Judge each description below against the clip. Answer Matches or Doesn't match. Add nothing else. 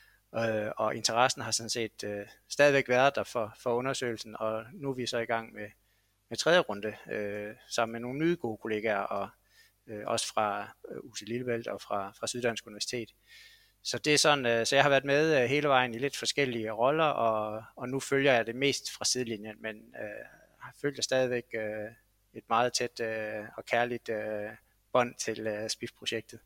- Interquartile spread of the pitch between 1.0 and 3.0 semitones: Matches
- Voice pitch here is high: Doesn't match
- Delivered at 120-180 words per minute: Doesn't match